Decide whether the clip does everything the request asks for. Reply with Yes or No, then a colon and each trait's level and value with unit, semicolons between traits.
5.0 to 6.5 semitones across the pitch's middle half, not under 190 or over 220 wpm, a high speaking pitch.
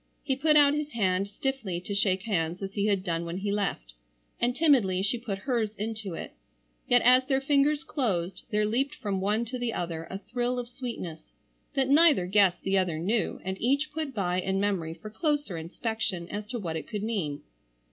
Yes: average, 5.3 semitones; average, 200 wpm; high, 210 Hz